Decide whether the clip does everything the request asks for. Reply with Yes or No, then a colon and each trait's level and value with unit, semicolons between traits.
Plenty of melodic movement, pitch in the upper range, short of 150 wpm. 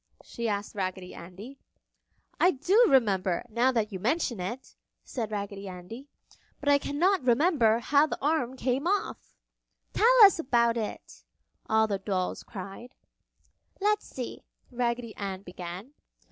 Yes: wide, 6.0 semitones; high, 235 Hz; average, 140 wpm